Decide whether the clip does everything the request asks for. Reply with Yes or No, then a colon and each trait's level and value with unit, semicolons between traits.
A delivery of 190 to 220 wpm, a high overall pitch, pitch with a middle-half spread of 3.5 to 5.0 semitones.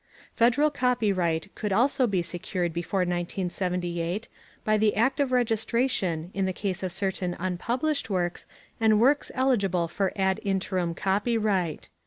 No: slow, 135 wpm; high, 195 Hz; average, 4.6 semitones